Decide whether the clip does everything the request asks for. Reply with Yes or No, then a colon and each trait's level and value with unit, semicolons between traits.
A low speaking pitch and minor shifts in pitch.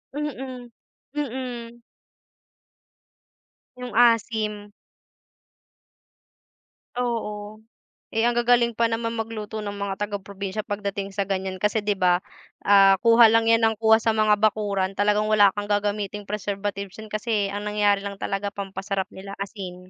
No: high, 210 Hz; narrow, 2.2 semitones